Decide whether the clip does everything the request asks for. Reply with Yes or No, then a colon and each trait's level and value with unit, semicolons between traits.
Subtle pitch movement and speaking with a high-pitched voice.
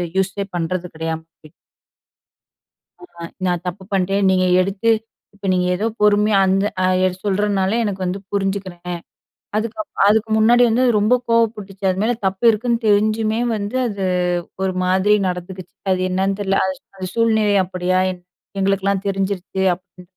Yes: narrow, 2.2 semitones; high, 195 Hz